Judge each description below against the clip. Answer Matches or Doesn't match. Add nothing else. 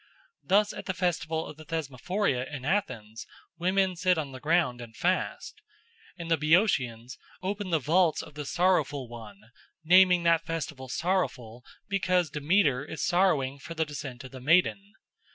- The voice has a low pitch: Doesn't match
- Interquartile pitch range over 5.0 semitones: Matches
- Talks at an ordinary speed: Matches